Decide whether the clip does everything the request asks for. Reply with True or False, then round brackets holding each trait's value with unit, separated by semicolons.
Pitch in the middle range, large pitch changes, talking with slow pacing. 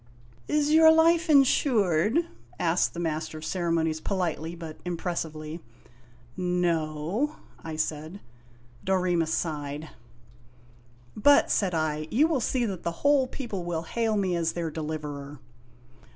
True (170 Hz; 5.7 semitones; 130 wpm)